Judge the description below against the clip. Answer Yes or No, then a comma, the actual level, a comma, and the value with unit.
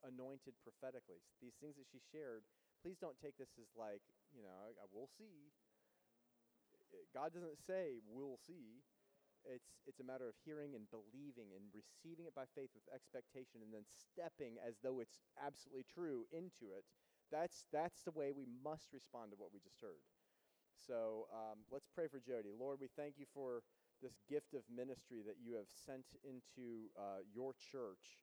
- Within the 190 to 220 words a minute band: No, average, 180 wpm